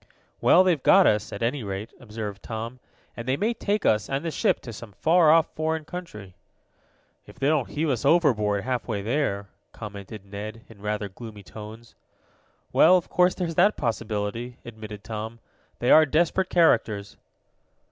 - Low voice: Yes, low, 115 Hz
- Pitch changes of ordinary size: No, wide, 6.9 semitones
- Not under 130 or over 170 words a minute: Yes, average, 165 wpm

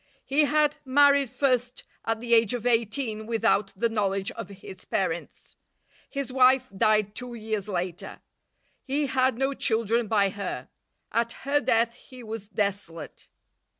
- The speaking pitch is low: No, high, 230 Hz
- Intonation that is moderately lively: Yes, average, 3.9 semitones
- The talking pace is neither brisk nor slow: Yes, average, 145 wpm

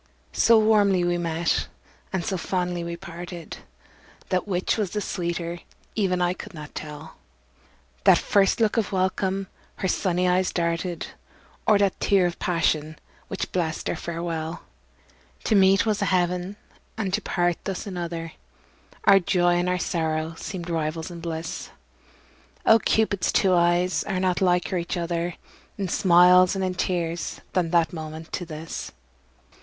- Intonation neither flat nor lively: No, narrow, 2.0 semitones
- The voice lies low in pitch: No, medium, 175 Hz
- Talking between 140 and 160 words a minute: Yes, average, 150 wpm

